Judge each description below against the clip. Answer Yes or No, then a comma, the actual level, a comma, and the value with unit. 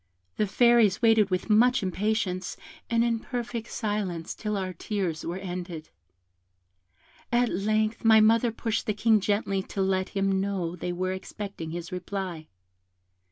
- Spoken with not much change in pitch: No, average, 3.2 semitones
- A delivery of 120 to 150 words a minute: Yes, average, 145 wpm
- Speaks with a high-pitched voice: Yes, high, 200 Hz